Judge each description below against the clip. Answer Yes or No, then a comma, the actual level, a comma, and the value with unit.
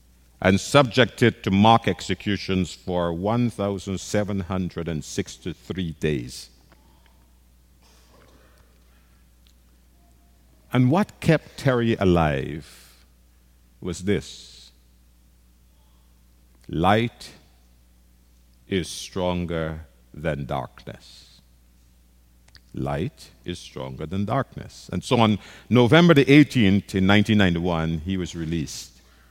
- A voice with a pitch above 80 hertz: No, very low, 75 Hz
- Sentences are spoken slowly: Yes, slow, 75 wpm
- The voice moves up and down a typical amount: No, wide, 8.2 semitones